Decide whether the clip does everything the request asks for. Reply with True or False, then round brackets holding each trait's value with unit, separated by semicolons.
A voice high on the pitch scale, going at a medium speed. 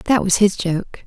False (195 Hz; 225 wpm)